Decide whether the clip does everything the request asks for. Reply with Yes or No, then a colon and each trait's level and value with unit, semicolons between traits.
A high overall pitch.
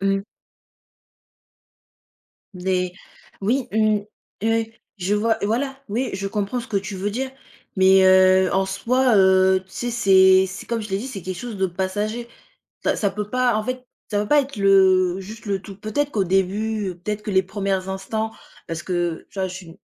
Yes: high, 195 Hz